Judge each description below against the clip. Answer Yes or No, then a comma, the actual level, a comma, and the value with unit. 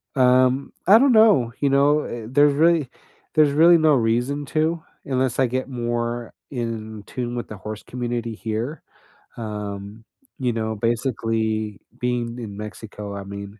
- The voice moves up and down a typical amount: Yes, average, 4.0 semitones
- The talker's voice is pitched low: Yes, low, 120 Hz